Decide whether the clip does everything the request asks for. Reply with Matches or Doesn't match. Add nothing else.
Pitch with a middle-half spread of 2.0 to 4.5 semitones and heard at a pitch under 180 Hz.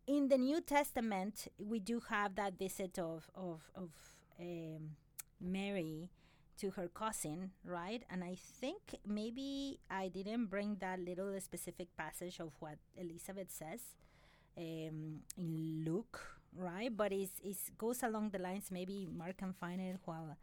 Doesn't match